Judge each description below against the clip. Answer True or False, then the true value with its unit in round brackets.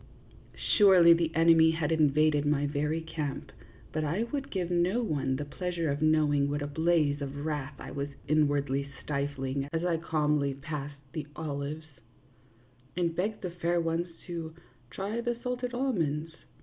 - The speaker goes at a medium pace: True (155 wpm)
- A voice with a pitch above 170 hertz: False (155 Hz)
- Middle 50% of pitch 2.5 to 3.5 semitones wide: True (3.1 semitones)